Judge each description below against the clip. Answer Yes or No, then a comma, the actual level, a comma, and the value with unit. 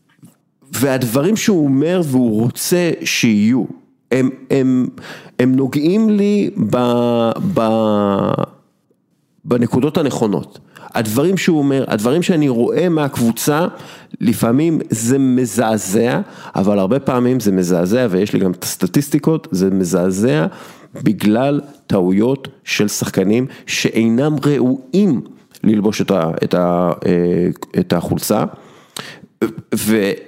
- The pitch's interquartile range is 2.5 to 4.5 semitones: No, average, 5.0 semitones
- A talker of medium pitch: No, low, 125 Hz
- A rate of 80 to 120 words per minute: Yes, average, 105 wpm